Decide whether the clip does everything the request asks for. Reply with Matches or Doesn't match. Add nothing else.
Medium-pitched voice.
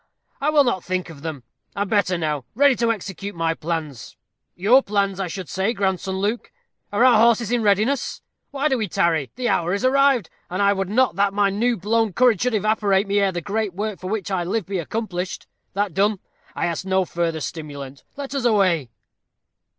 Doesn't match